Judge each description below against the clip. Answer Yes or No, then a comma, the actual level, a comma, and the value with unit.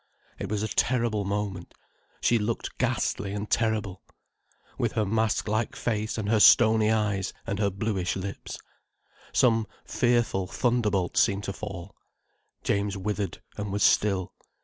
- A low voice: Yes, low, 105 Hz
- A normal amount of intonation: No, narrow, 2.0 semitones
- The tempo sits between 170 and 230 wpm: No, average, 140 wpm